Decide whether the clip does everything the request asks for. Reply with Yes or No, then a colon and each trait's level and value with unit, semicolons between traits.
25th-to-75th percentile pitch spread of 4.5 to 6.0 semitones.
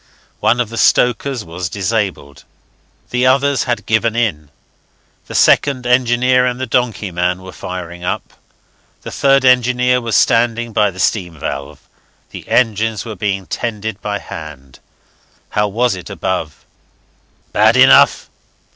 Yes: average, 5.1 semitones